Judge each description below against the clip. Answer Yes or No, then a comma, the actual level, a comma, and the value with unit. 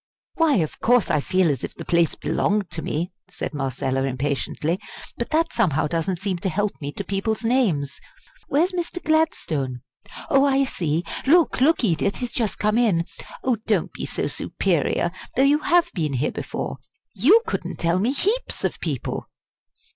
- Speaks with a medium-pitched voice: No, high, 200 Hz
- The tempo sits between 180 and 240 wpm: No, average, 170 wpm